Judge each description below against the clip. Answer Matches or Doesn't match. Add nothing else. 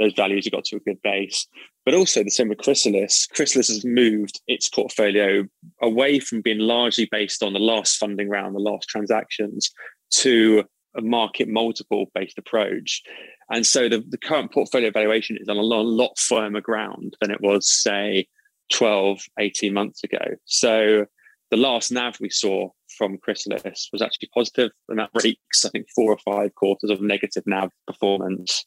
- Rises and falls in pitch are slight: Matches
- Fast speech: Doesn't match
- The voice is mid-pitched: Doesn't match